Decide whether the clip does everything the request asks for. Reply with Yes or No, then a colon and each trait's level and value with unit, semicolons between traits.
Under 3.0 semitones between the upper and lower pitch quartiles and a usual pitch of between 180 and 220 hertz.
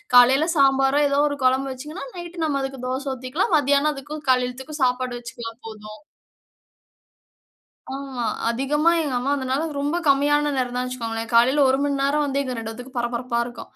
No: narrow, 2.5 semitones; very high, 270 Hz